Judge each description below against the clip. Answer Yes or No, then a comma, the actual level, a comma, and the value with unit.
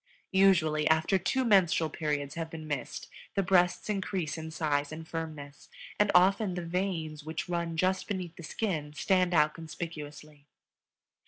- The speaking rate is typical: Yes, average, 150 wpm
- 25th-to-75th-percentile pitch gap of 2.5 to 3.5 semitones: Yes, average, 3.2 semitones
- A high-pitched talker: No, medium, 165 Hz